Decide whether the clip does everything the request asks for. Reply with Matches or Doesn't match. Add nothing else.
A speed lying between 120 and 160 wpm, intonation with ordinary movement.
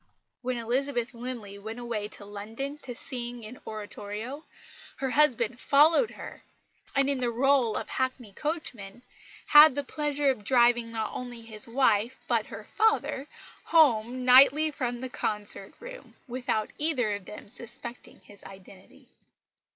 Matches